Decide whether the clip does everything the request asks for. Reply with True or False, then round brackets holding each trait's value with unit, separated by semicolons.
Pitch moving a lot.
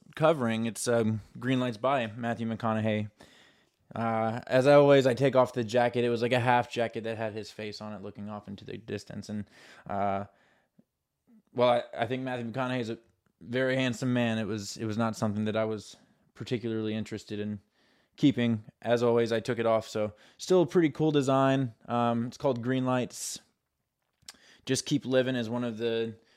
False (2.7 semitones)